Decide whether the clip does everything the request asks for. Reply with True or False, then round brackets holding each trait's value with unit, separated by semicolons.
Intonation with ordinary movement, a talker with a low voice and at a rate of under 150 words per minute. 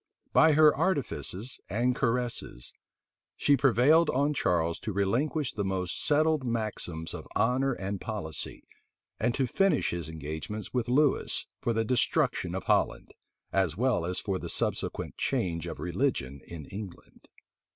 False (7.0 semitones; 110 Hz; 140 wpm)